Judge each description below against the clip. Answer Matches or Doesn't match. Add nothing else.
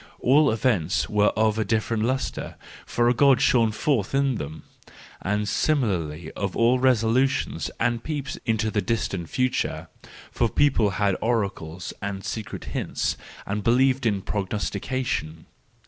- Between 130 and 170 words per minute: Matches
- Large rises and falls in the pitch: Doesn't match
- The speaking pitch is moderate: Doesn't match